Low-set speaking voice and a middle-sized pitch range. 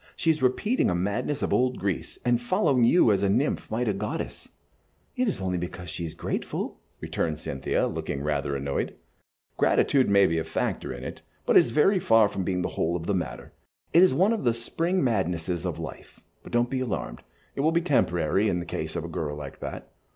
No: low, 105 Hz; wide, 7.3 semitones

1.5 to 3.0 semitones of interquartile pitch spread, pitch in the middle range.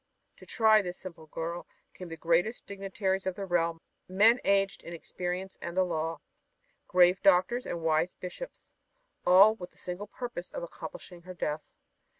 Yes: narrow, 2.6 semitones; medium, 180 Hz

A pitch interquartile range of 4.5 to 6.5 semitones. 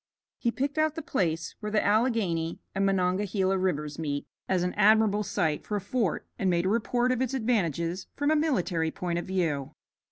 Yes: average, 5.2 semitones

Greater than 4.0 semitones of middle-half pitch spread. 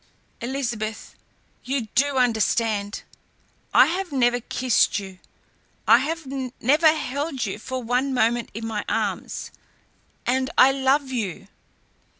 No: average, 3.5 semitones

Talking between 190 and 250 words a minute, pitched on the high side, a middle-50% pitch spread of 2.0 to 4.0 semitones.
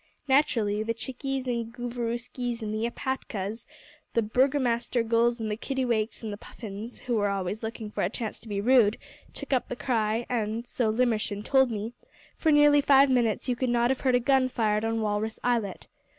Yes: average, 195 wpm; high, 235 Hz; narrow, 2.6 semitones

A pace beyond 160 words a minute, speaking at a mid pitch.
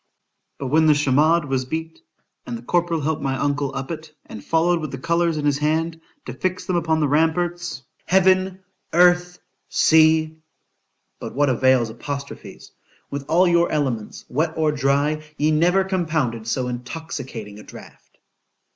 No: average, 145 wpm; medium, 155 Hz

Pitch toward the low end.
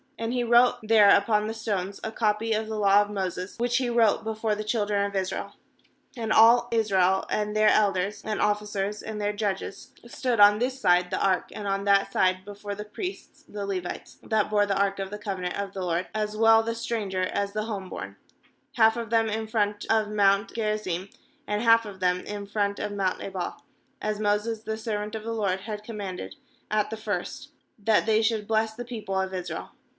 No: high, 210 Hz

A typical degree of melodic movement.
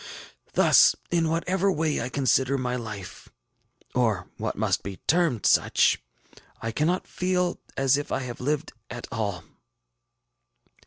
No: wide, 5.9 semitones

